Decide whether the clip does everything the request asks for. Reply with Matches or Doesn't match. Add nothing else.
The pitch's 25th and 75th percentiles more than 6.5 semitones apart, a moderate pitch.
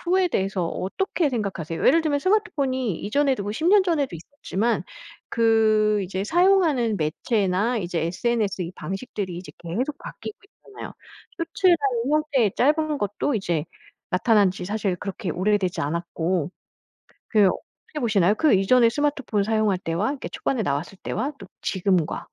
Doesn't match